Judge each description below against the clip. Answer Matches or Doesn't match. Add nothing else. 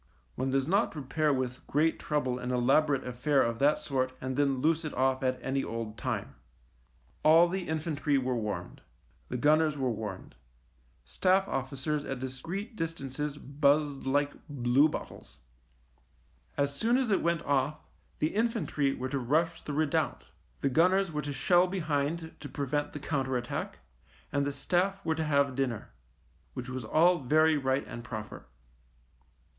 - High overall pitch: Doesn't match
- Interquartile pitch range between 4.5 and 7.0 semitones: Doesn't match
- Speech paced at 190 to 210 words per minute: Doesn't match